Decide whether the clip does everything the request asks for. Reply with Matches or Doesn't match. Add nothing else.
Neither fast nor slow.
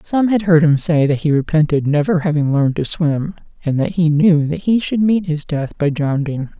Doesn't match